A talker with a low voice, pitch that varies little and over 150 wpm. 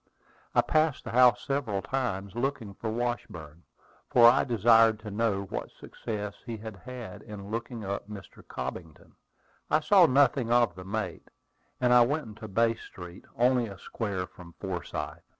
No: low, 115 Hz; average, 3.8 semitones; average, 160 wpm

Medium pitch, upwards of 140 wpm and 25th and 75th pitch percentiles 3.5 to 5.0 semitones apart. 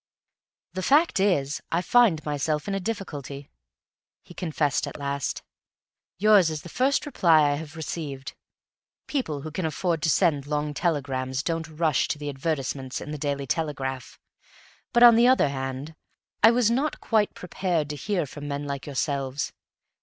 Yes: medium, 155 Hz; average, 160 wpm; average, 4.7 semitones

